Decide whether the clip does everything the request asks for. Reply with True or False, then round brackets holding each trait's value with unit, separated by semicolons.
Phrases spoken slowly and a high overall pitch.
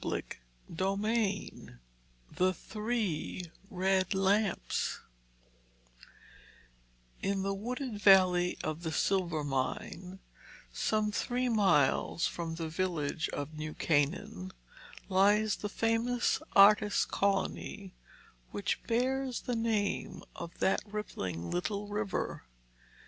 True (95 wpm; 195 Hz)